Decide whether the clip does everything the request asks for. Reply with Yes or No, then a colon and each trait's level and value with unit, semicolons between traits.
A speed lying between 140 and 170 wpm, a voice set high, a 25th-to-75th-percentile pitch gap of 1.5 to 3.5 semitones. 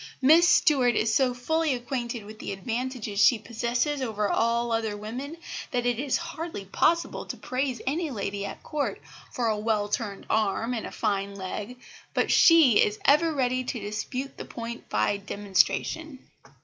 No: average, 165 wpm; high, 240 Hz; average, 4.3 semitones